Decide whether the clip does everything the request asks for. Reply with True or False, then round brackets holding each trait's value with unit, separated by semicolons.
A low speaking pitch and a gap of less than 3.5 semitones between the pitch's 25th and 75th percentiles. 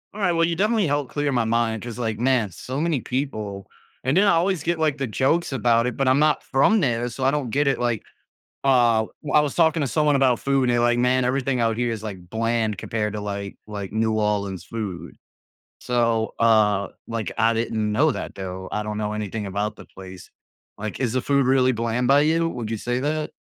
False (120 Hz; 4.3 semitones)